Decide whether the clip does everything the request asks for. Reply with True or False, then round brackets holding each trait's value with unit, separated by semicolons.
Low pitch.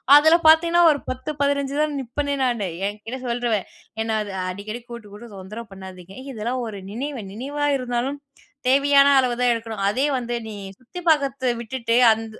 False (245 Hz)